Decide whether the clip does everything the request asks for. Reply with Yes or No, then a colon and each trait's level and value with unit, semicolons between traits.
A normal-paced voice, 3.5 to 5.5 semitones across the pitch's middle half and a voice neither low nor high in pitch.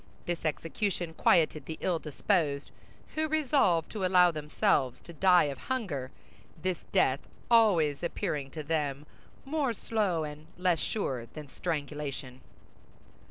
No: slow, 120 wpm; average, 4.4 semitones; medium, 165 Hz